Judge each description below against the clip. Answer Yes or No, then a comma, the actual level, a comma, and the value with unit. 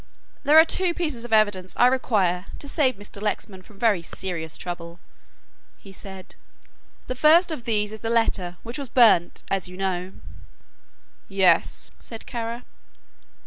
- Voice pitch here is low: No, high, 210 Hz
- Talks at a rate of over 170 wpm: No, average, 150 wpm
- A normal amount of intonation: Yes, average, 4.9 semitones